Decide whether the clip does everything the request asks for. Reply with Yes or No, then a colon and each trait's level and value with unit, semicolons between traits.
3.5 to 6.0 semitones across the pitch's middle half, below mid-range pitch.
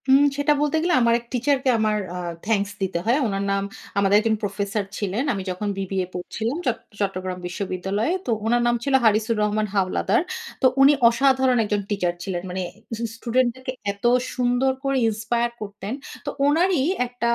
No: average, 4.2 semitones; high, 220 Hz